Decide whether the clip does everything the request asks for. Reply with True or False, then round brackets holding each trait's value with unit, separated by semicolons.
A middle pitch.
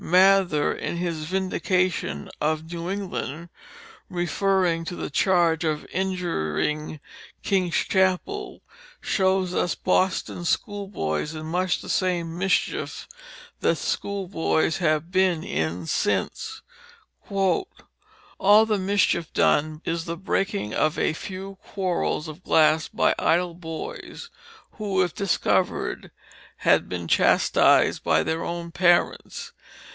True (175 Hz)